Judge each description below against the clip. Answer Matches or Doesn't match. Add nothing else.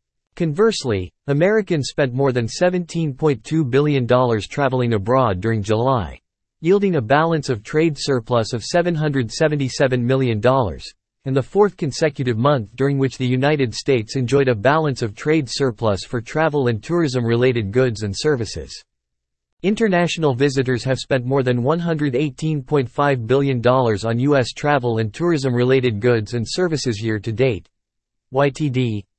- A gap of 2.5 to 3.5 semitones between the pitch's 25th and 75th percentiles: Doesn't match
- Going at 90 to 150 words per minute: Matches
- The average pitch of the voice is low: Matches